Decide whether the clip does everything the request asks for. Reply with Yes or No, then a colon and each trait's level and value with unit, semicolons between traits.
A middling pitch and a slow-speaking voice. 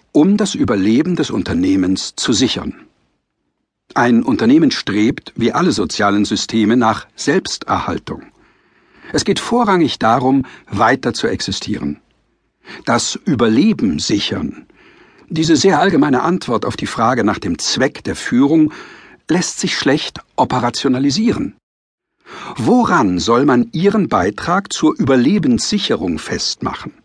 Yes: medium, 160 Hz; slow, 110 wpm